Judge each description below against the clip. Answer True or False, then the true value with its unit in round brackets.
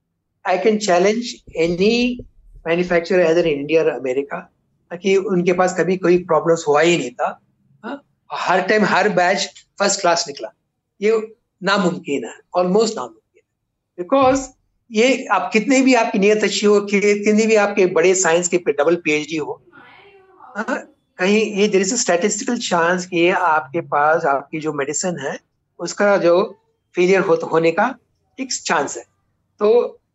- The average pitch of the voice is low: False (185 Hz)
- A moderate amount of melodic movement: True (4.4 semitones)